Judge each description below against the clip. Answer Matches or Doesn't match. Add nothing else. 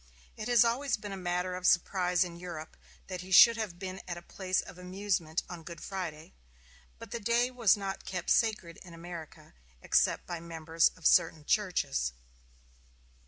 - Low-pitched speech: Doesn't match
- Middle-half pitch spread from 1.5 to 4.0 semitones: Matches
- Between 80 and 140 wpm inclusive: Doesn't match